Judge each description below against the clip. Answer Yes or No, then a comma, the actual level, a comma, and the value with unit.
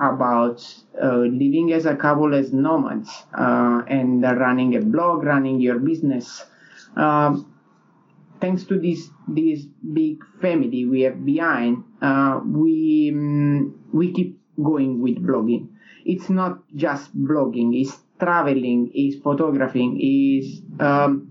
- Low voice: No, medium, 145 Hz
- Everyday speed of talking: No, slow, 125 wpm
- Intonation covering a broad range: No, average, 4.2 semitones